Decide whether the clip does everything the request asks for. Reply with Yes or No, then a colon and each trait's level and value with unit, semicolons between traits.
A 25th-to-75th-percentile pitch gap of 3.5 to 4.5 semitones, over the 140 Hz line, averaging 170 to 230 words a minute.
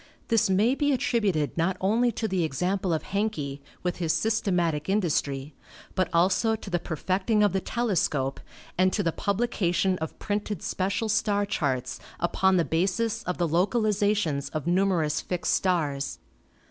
No: average, 4.2 semitones; medium, 185 Hz; average, 150 wpm